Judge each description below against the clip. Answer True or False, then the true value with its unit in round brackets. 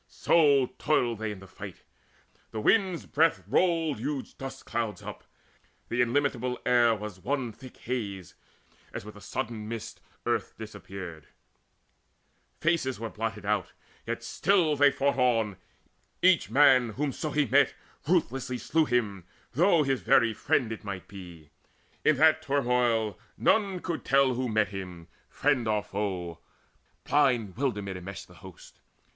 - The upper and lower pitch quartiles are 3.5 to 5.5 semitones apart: True (5.2 semitones)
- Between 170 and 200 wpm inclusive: False (140 wpm)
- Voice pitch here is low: True (120 Hz)